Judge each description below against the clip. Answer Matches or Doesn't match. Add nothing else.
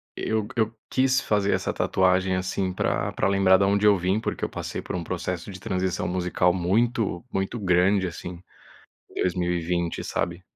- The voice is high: Doesn't match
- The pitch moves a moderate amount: Doesn't match